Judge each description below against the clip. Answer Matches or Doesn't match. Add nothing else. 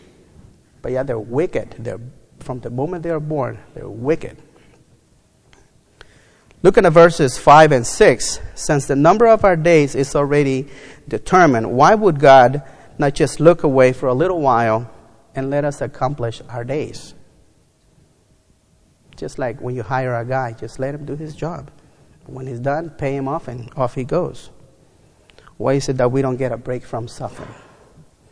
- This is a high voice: Doesn't match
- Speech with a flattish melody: Doesn't match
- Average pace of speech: Matches